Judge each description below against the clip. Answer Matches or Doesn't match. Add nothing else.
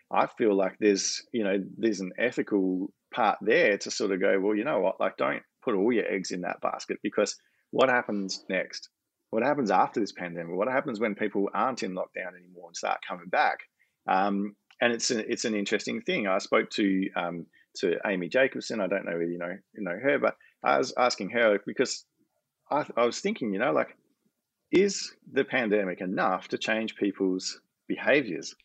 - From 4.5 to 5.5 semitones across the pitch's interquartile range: Doesn't match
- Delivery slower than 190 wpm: Doesn't match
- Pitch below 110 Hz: Matches